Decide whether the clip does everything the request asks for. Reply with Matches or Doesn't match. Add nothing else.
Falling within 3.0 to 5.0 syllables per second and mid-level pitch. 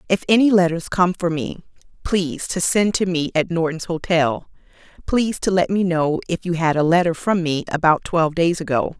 Doesn't match